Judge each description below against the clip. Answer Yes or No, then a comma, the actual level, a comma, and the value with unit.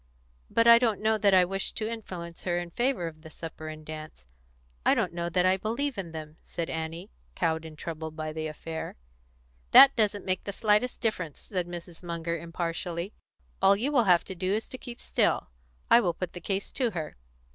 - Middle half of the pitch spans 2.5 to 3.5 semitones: No, average, 4.5 semitones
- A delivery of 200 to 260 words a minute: Yes, fast, 205 wpm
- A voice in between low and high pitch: Yes, medium, 175 Hz